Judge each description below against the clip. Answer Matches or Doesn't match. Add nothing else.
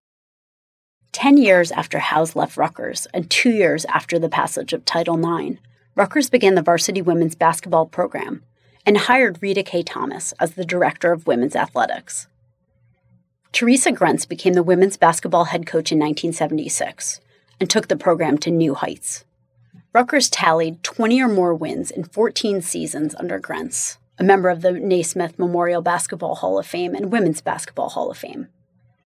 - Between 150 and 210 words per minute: Matches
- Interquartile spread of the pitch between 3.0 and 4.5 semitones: Matches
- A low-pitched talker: Doesn't match